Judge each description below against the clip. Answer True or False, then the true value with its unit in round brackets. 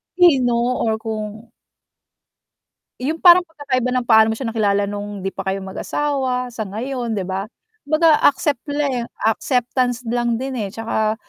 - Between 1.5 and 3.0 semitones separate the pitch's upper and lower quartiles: False (3.7 semitones)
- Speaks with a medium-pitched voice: False (240 Hz)